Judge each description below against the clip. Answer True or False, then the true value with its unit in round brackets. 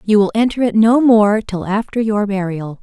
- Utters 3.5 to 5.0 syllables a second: True (4.8 syllables/s)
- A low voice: False (210 Hz)